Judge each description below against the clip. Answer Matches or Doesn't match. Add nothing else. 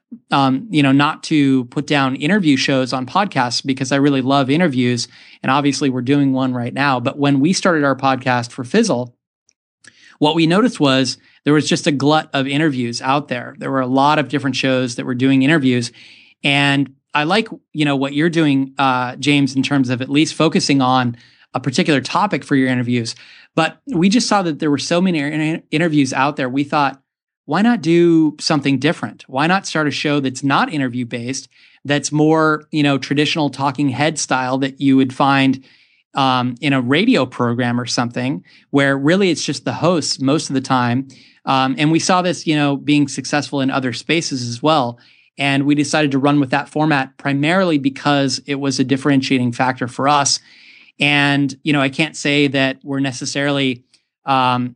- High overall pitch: Doesn't match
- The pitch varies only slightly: Matches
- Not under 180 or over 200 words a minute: Matches